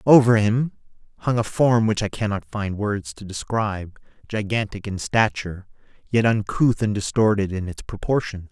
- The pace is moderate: Yes, average, 150 wpm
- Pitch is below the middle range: Yes, low, 105 Hz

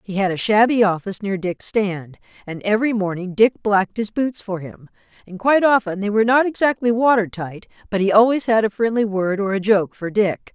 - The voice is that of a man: No, female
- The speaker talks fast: Yes, fast, 215 wpm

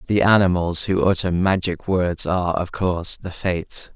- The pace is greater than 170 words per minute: No, average, 165 wpm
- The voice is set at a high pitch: No, very low, 90 Hz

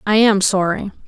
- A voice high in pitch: Yes, high, 200 Hz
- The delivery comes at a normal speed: Yes, average, 170 wpm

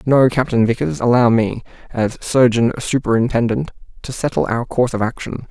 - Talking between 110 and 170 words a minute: Yes, average, 155 wpm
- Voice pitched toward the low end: Yes, low, 120 Hz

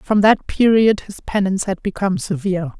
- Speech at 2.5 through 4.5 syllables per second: No, 5.5 syllables/s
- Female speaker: Yes, female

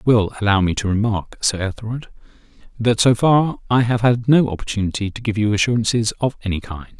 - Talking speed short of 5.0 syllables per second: No, 6.0 syllables/s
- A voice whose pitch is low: Yes, low, 110 Hz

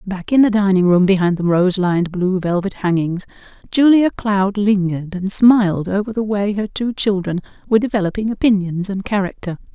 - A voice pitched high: Yes, high, 195 Hz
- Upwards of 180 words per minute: No, average, 170 wpm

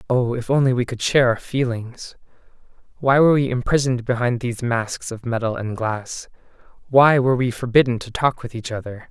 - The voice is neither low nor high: No, low, 125 Hz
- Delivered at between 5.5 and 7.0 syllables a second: Yes, 5.6 syllables/s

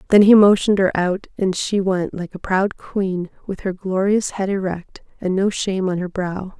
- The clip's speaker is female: Yes, female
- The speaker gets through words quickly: Yes, fast, 210 wpm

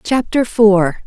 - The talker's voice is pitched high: Yes, high, 215 Hz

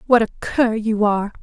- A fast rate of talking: Yes, fast, 210 wpm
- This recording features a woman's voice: Yes, female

